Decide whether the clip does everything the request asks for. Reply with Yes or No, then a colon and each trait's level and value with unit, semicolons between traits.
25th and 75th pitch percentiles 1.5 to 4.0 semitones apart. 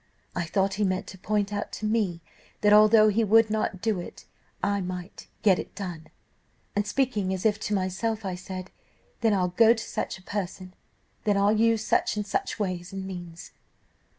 Yes: narrow, 2.5 semitones